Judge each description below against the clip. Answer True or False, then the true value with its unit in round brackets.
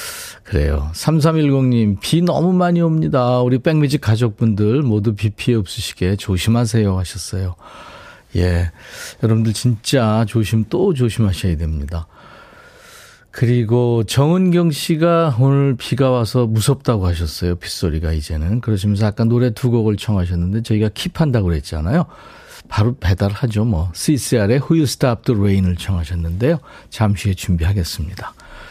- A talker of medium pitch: False (110 Hz)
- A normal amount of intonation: False (5.8 semitones)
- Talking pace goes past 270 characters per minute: True (335 characters per minute)